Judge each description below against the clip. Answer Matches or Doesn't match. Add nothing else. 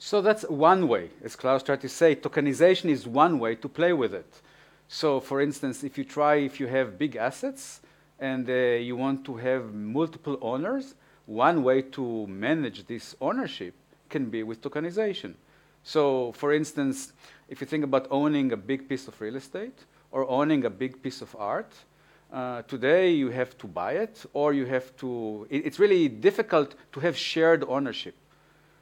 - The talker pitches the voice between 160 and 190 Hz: Doesn't match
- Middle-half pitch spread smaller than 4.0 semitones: Matches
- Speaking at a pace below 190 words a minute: Matches